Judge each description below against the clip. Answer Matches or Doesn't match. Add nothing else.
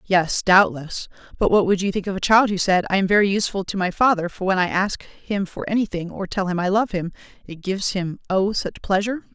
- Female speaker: Matches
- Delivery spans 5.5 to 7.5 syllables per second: Matches